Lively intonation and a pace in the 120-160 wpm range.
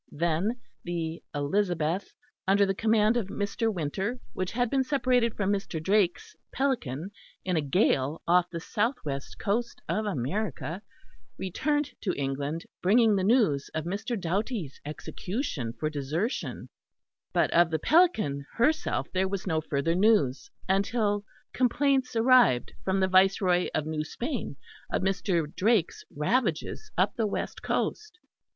Yes: wide, 6.0 semitones; average, 140 wpm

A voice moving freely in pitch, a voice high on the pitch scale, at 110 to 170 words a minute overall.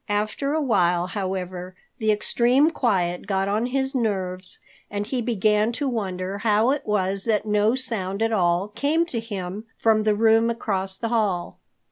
No: average, 3.4 semitones; high, 210 Hz; average, 165 wpm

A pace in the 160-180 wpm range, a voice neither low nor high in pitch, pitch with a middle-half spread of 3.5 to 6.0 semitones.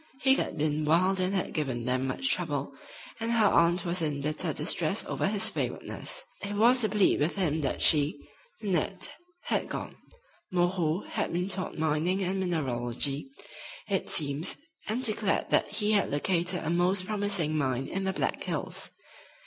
Yes: average, 165 wpm; medium, 175 Hz; average, 4.7 semitones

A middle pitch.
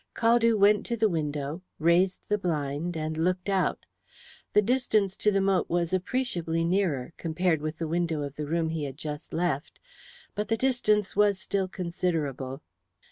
Yes: medium, 175 Hz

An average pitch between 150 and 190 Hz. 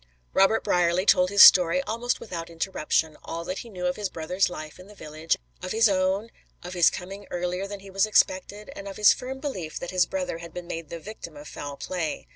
Yes: medium, 185 Hz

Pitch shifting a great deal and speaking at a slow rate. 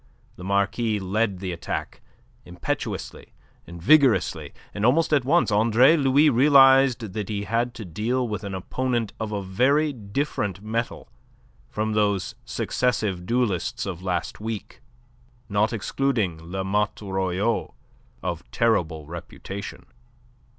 No: average, 4.5 semitones; slow, 125 wpm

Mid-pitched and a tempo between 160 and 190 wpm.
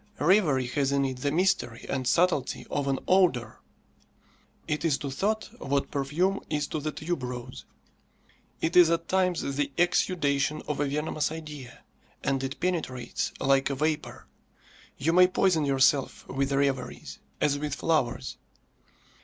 No: medium, 145 Hz; average, 145 wpm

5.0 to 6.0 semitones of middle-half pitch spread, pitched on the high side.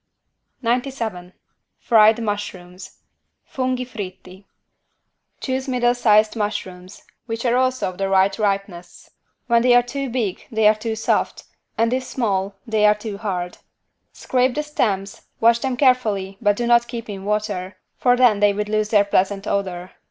No: average, 3.6 semitones; high, 215 Hz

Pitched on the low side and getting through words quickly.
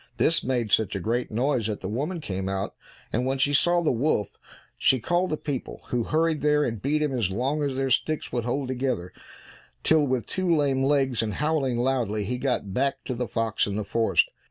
Yes: low, 130 Hz; fast, 215 wpm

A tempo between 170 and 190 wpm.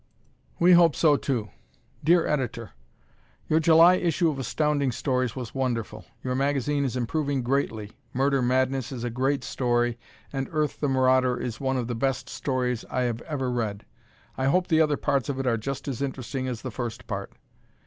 Yes: average, 180 wpm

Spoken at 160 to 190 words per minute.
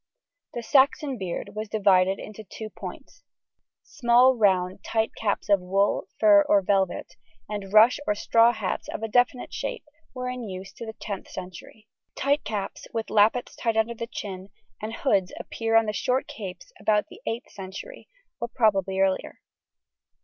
Yes: average, 165 wpm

